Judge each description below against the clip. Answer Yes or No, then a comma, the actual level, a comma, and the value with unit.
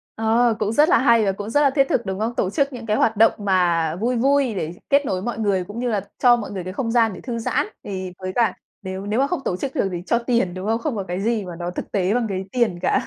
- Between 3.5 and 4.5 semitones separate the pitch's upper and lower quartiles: Yes, average, 4.2 semitones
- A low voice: No, high, 220 Hz